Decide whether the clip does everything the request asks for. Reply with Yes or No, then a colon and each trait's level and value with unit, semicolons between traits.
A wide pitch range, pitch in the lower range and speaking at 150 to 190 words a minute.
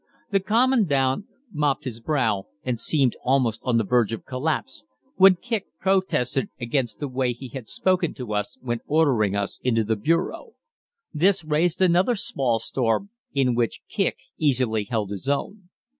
Yes: wide, 6.8 semitones; low, 130 Hz; average, 160 wpm